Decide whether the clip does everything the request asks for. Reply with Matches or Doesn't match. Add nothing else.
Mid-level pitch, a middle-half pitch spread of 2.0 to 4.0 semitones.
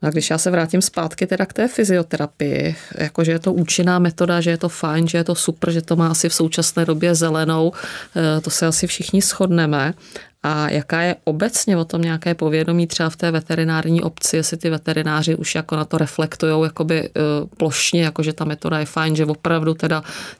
Doesn't match